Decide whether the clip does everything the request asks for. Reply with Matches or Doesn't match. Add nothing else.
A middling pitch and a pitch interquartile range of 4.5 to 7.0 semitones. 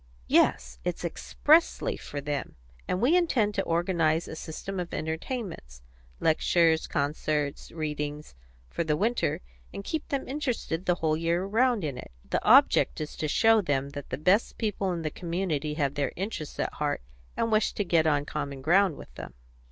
Matches